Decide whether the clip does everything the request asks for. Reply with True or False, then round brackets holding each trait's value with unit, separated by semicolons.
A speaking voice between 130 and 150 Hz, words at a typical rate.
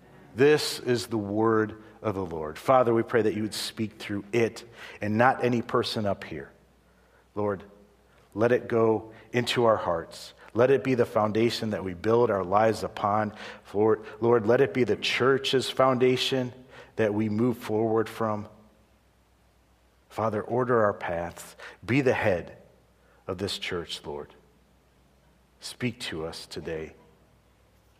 False (110 Hz; 145 wpm)